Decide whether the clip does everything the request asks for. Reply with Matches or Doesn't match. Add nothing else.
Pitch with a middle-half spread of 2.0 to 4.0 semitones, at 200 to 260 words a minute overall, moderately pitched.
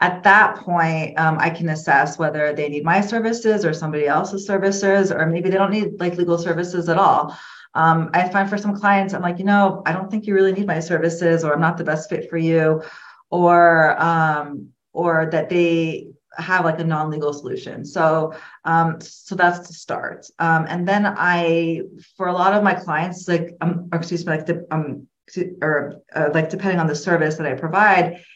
Matches